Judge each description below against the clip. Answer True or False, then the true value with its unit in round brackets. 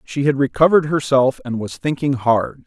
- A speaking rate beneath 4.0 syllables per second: False (5.1 syllables/s)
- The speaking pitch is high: False (135 Hz)